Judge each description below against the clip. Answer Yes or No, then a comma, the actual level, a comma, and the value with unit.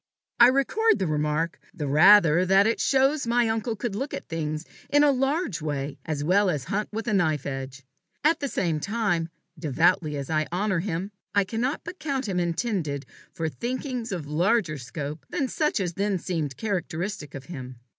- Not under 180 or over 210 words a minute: Yes, average, 185 wpm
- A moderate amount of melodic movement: No, wide, 7.2 semitones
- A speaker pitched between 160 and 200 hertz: Yes, medium, 185 Hz